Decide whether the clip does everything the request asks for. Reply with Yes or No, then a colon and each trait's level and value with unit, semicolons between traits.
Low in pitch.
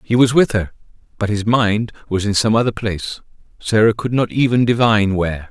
Yes: low, 110 Hz